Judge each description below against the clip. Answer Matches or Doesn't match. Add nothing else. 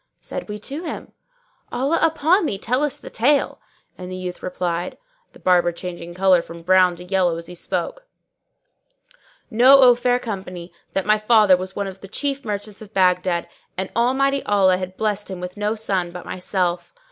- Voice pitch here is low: Doesn't match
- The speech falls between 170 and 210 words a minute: Matches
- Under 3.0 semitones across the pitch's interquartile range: Doesn't match